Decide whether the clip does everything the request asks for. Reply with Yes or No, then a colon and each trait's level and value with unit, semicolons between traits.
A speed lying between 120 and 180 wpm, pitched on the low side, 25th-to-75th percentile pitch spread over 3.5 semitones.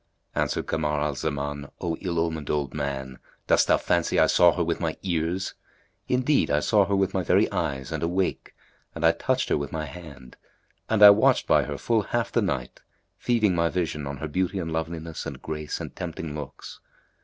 No: average, 200 wpm; very low, 80 Hz; average, 4.3 semitones